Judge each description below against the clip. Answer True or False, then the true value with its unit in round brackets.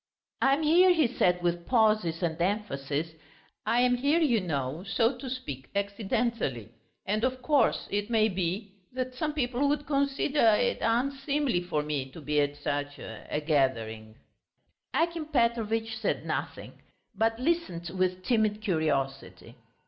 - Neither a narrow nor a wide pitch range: False (7.9 semitones)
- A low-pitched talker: False (215 Hz)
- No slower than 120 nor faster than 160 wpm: True (145 wpm)